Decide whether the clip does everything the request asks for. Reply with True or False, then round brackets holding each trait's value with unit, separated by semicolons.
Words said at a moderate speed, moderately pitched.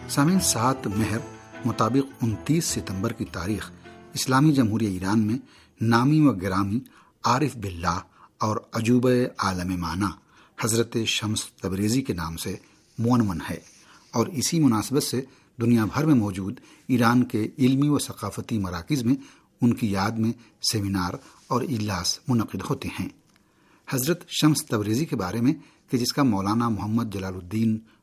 False (140 wpm; 115 Hz)